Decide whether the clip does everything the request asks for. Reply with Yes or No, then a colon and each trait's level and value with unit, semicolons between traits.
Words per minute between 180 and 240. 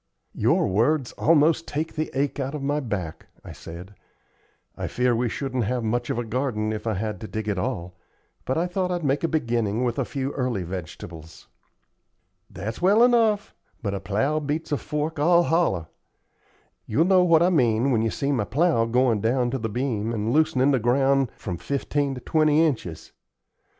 Yes: average, 190 wpm